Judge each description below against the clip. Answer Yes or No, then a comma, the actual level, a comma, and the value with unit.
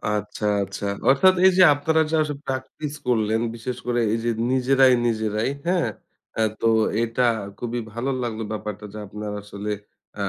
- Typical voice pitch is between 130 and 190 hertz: No, low, 120 Hz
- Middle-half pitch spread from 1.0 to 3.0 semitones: No, average, 3.7 semitones